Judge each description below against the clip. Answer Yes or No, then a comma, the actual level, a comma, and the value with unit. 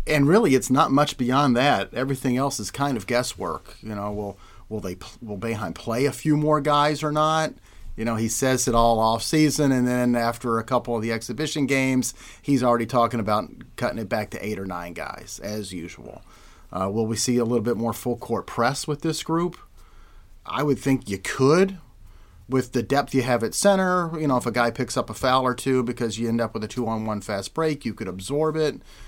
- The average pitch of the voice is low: Yes, low, 120 Hz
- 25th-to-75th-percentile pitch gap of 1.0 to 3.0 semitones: No, average, 4.2 semitones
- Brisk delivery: Yes, fast, 225 wpm